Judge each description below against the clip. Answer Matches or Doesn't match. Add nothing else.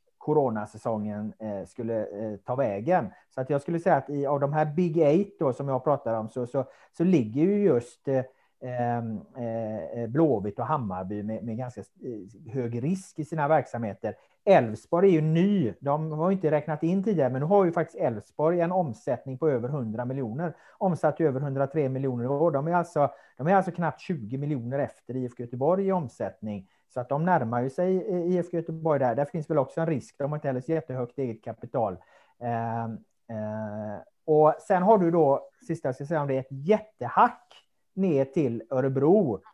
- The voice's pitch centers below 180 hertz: Matches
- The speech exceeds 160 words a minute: Matches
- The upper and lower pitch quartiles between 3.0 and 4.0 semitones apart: Doesn't match